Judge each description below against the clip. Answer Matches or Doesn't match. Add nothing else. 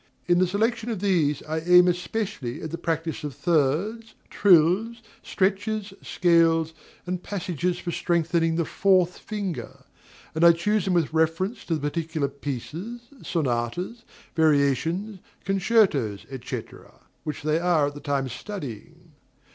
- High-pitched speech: Doesn't match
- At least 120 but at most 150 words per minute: Matches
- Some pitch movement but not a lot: Matches